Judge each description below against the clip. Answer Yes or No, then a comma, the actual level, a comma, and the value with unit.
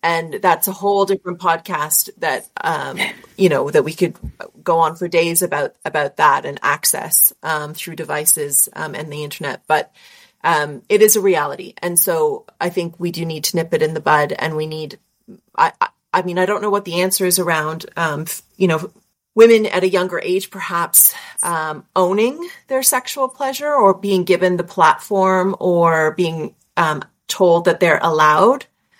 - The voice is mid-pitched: Yes, medium, 180 Hz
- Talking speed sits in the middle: Yes, average, 180 wpm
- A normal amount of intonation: Yes, average, 4.2 semitones